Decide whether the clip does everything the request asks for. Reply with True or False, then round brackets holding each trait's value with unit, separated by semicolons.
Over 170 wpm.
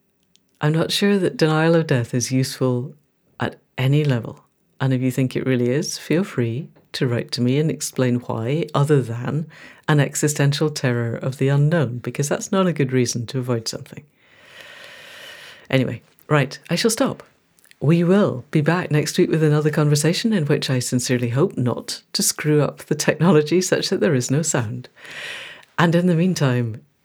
True (180 wpm)